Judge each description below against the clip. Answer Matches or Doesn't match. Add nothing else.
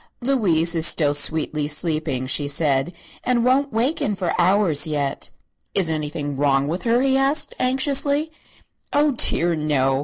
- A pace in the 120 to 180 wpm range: Matches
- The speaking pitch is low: Doesn't match